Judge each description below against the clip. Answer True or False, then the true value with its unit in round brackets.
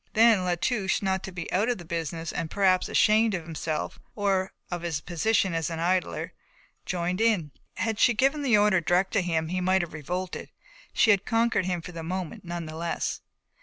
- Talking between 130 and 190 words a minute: False (205 wpm)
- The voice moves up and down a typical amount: True (3.4 semitones)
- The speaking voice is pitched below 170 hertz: False (185 Hz)